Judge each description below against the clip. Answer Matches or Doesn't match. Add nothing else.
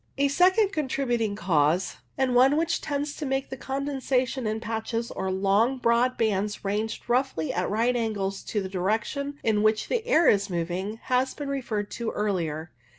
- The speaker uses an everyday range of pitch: Matches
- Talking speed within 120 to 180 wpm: Matches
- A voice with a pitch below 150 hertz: Doesn't match